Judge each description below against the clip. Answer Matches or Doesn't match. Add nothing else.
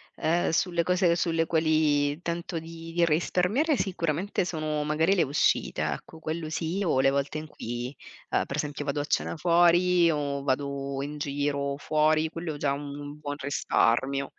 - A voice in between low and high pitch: Matches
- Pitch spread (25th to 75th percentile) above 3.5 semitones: Doesn't match